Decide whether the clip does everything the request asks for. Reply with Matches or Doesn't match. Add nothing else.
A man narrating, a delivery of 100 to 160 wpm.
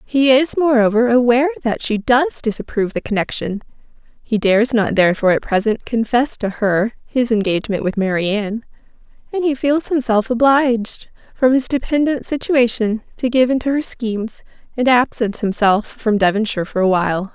Doesn't match